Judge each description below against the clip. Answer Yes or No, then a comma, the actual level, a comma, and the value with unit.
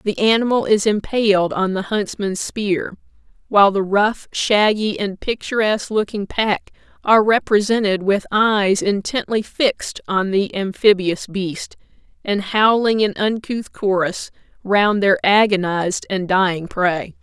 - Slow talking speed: Yes, slow, 130 wpm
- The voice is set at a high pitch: Yes, high, 200 Hz